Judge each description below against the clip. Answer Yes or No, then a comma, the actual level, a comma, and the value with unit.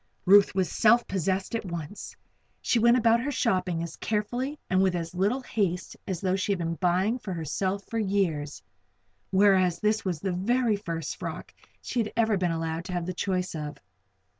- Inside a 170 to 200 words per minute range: Yes, average, 190 wpm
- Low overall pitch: No, high, 190 Hz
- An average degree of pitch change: Yes, average, 3.6 semitones